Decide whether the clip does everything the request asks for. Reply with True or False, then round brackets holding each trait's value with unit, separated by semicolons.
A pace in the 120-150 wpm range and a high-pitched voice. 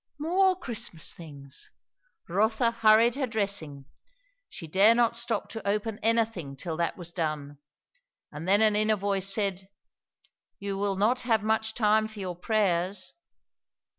True (140 wpm; 205 Hz)